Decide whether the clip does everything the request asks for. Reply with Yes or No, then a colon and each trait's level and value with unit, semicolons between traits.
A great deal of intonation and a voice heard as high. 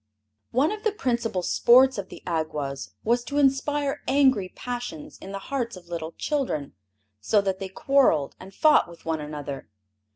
Yes: wide, 8.4 semitones; high, 210 Hz